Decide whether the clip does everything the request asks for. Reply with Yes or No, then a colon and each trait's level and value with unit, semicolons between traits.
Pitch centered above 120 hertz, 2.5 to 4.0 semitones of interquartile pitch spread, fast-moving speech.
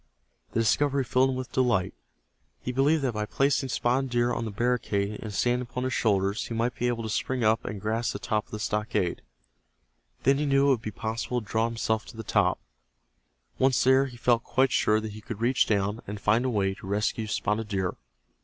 No: low, 115 Hz; average, 3.1 semitones; fast, 220 wpm